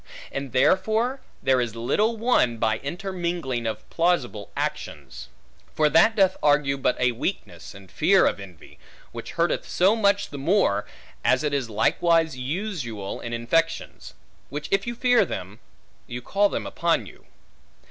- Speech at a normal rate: Yes, average, 150 wpm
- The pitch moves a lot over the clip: Yes, wide, 8.2 semitones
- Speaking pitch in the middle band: Yes, medium, 145 Hz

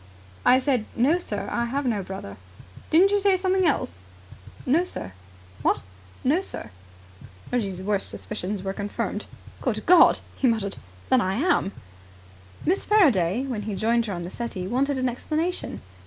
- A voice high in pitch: Yes, high, 240 Hz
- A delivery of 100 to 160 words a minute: Yes, average, 155 wpm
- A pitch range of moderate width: No, wide, 7.7 semitones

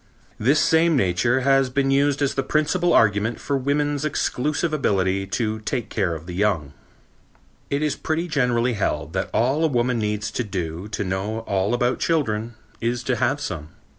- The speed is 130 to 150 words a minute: No, average, 175 wpm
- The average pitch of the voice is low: Yes, low, 120 Hz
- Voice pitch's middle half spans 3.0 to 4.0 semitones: No, wide, 5.6 semitones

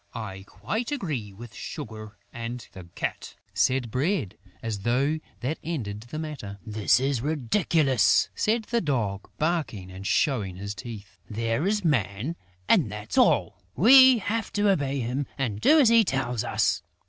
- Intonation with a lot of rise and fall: Yes, wide, 7.2 semitones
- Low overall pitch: Yes, low, 125 Hz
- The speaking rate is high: No, average, 155 wpm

